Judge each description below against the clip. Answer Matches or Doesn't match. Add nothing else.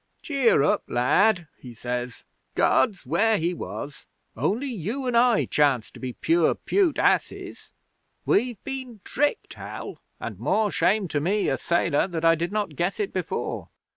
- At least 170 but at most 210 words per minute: Doesn't match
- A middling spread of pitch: Doesn't match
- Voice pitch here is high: Matches